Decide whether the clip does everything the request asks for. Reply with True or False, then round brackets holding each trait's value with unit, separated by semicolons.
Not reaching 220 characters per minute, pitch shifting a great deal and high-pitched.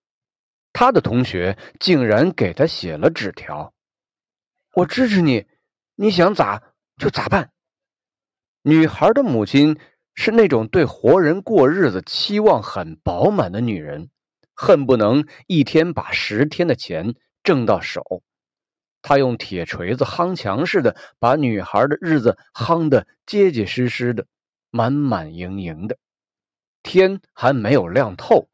False (190 characters per minute; 8.0 semitones; 135 Hz)